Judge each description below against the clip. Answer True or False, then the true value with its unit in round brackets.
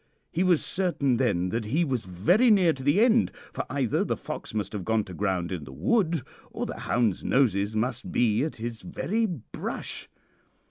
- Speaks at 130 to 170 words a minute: False (190 wpm)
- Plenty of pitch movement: True (8.3 semitones)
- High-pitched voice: False (120 Hz)